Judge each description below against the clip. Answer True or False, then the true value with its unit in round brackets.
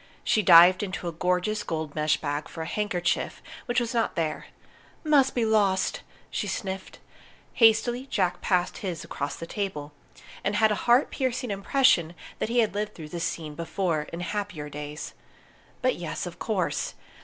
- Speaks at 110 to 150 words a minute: False (165 wpm)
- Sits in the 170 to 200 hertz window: True (190 Hz)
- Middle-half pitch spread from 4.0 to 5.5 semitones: True (4.9 semitones)